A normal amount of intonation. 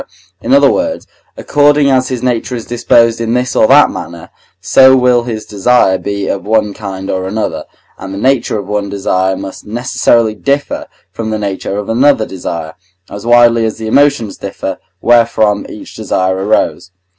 Yes: average, 3.9 semitones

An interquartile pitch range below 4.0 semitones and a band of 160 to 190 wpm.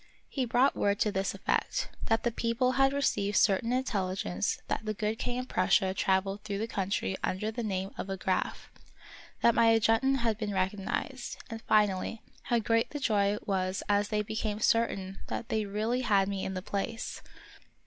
Yes: average, 3.0 semitones; average, 180 wpm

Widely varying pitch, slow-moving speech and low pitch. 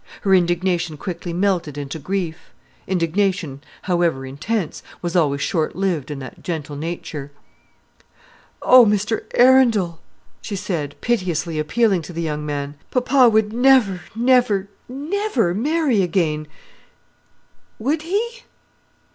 No: wide, 6.3 semitones; slow, 115 wpm; medium, 185 Hz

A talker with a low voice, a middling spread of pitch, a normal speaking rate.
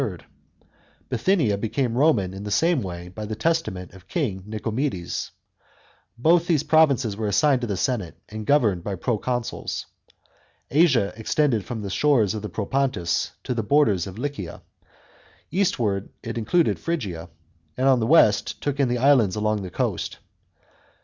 No: low, 115 Hz; wide, 5.9 semitones; average, 150 wpm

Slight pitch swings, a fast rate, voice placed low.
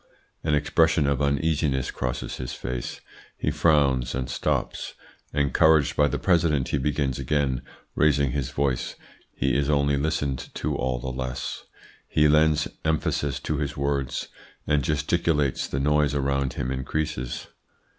No: narrow, 2.2 semitones; average, 140 wpm; very low, 70 Hz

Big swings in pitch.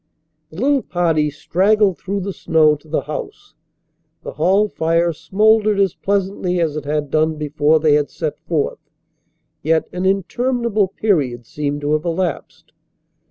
No: average, 4.5 semitones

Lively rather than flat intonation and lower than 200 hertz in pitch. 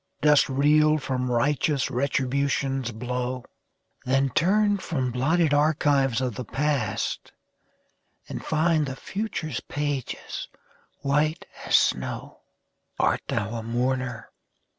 No: average, 3.2 semitones; low, 135 Hz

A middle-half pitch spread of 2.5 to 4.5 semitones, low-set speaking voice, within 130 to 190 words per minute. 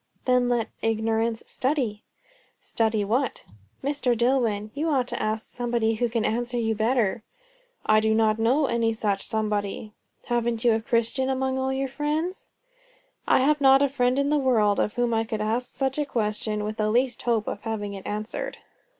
No: average, 3.2 semitones; high, 235 Hz; average, 180 wpm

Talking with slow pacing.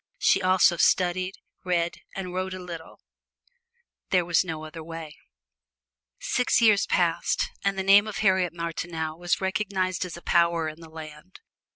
No: average, 155 wpm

